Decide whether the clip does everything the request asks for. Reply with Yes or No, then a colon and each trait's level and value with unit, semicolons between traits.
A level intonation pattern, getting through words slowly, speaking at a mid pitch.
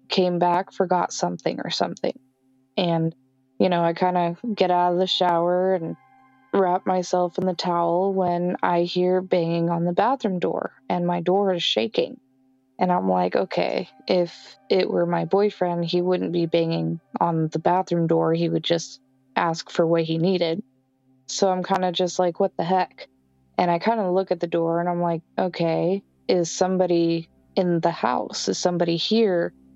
No: narrow, 1.9 semitones; average, 180 wpm; medium, 175 Hz